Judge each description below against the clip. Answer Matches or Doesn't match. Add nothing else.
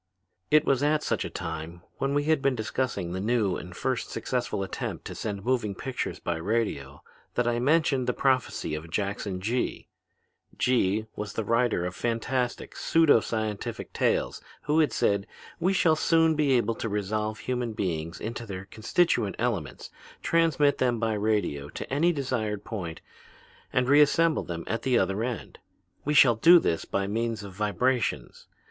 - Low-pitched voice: Matches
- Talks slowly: Doesn't match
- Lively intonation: Doesn't match